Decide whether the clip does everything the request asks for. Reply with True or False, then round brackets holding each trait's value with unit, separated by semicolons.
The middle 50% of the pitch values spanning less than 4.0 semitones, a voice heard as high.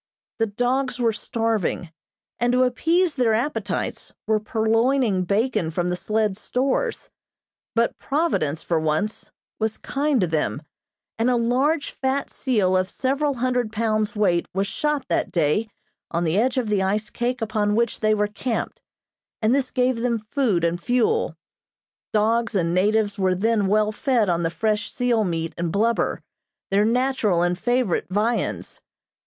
False (4.3 semitones; 220 Hz)